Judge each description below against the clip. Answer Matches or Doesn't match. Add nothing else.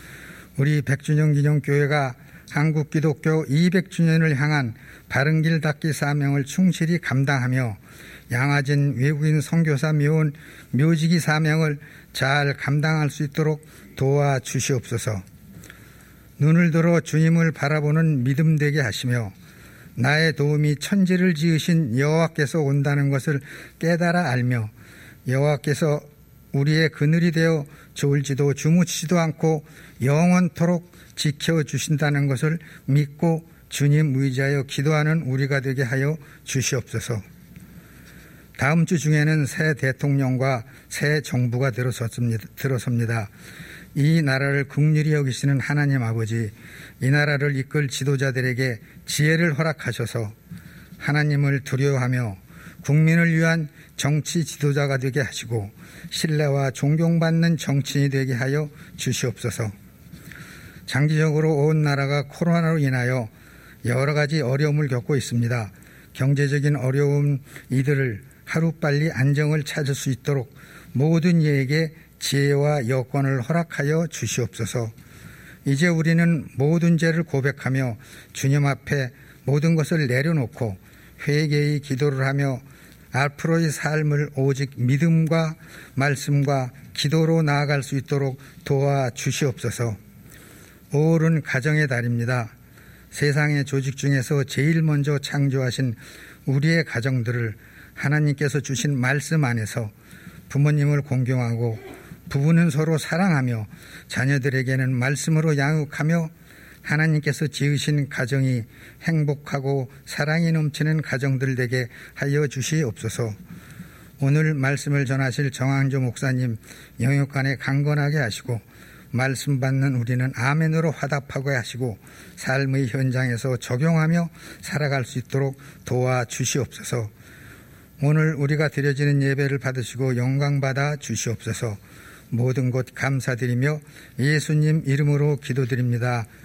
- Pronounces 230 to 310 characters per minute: Matches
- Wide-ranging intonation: Doesn't match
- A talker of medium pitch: Matches